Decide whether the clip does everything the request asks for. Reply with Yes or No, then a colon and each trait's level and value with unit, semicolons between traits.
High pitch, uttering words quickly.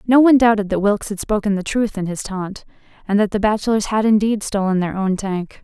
Yes: high, 205 Hz; fast, 235 wpm